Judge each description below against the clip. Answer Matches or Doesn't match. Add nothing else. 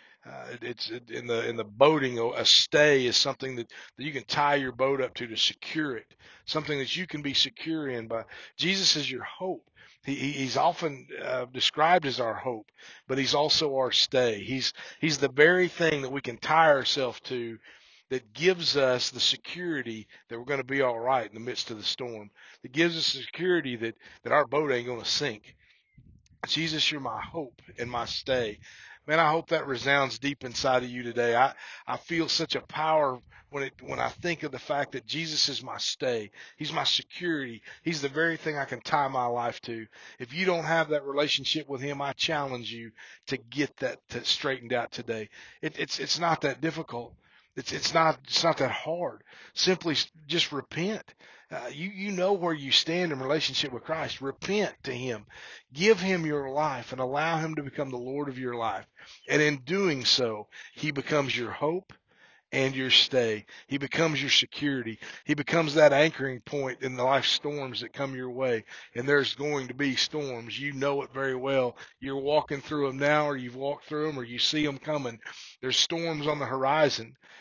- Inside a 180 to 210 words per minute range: Matches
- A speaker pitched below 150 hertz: Matches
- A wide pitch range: Doesn't match